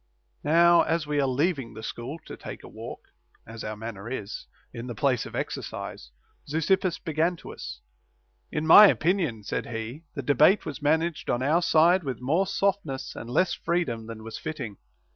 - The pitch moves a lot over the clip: Yes, wide, 6.4 semitones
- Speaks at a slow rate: No, average, 185 wpm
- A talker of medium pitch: Yes, medium, 145 Hz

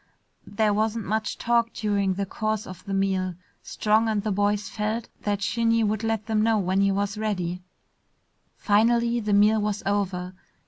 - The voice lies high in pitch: Yes, high, 210 Hz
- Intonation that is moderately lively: No, narrow, 1.8 semitones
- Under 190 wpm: Yes, average, 170 wpm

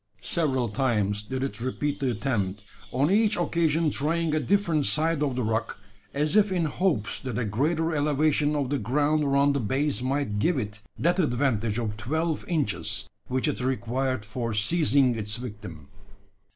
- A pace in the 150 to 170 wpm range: Yes, average, 165 wpm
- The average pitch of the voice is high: No, low, 135 Hz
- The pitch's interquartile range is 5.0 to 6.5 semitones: Yes, average, 5.3 semitones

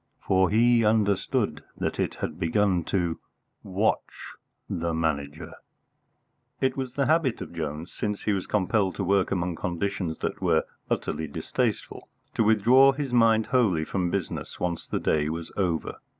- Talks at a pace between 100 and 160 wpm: Yes, average, 155 wpm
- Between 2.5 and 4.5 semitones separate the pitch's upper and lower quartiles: No, average, 4.9 semitones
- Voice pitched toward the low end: Yes, very low, 95 Hz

